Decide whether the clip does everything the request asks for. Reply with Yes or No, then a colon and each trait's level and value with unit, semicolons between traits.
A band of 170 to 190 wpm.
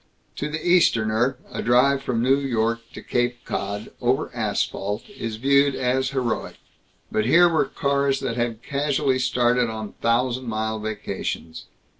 No: average, 145 wpm